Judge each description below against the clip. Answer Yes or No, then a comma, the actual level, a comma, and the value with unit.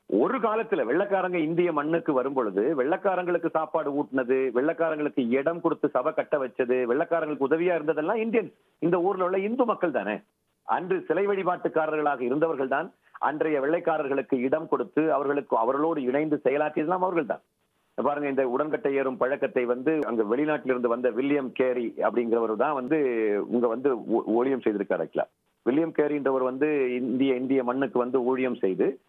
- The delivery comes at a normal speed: No, fast, 140 wpm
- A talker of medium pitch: Yes, medium, 150 Hz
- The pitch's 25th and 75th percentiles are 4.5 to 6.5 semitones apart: No, average, 4.0 semitones